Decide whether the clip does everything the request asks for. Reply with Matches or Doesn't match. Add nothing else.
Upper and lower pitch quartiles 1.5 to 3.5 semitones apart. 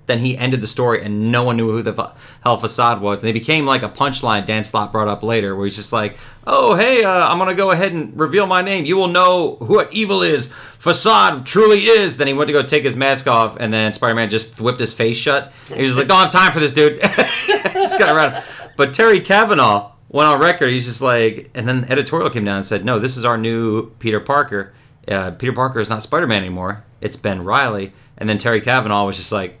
Doesn't match